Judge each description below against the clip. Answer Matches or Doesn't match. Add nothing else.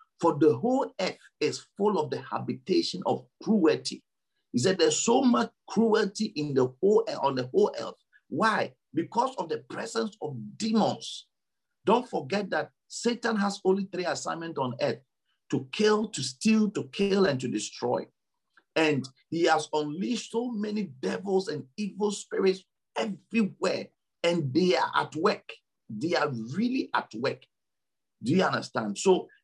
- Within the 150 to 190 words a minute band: Matches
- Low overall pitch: Doesn't match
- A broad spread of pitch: Matches